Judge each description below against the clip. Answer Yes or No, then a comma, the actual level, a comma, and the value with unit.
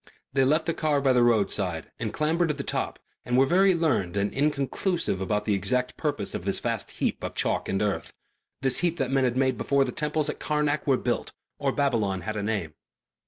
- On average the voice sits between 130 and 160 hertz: Yes, low, 135 Hz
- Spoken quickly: Yes, fast, 215 wpm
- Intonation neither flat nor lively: No, wide, 6.1 semitones